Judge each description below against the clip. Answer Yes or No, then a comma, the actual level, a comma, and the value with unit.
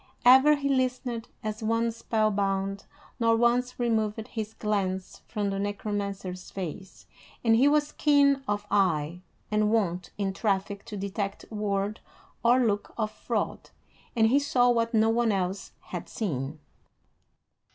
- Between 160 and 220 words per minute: No, average, 140 wpm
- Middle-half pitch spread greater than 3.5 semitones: No, average, 3.2 semitones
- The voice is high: Yes, high, 215 Hz